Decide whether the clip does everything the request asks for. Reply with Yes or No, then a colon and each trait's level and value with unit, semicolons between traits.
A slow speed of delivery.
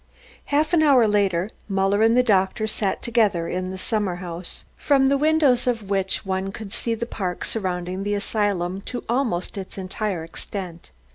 No: average, 170 wpm